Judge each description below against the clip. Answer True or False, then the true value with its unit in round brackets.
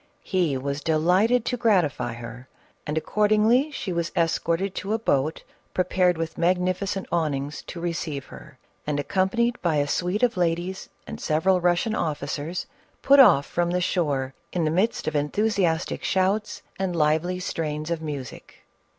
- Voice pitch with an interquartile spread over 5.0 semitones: False (3.9 semitones)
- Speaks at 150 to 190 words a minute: True (155 wpm)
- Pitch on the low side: False (175 Hz)